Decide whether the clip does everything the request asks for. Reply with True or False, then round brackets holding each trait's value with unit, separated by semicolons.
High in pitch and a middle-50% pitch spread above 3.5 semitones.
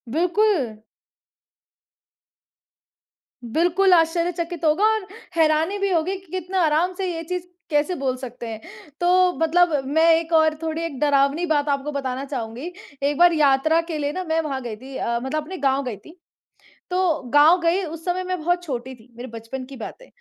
True (315 Hz; 4.4 semitones)